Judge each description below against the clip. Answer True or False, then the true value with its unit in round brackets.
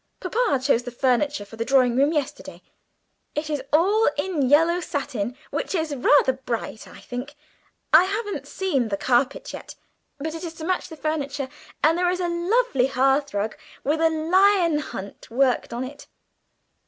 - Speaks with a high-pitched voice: True (290 Hz)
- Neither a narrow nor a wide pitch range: True (4.9 semitones)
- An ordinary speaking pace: True (165 wpm)